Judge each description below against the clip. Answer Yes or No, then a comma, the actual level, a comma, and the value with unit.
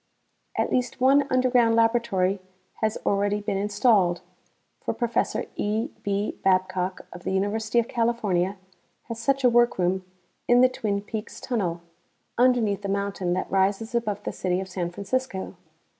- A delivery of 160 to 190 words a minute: No, average, 145 wpm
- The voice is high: Yes, high, 205 Hz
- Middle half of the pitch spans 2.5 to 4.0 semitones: Yes, average, 3.7 semitones